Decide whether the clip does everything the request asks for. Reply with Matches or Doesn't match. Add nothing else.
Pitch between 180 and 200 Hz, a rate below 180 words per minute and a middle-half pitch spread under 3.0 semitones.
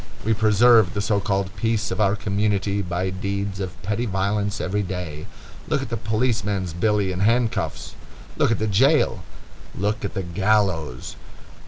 Doesn't match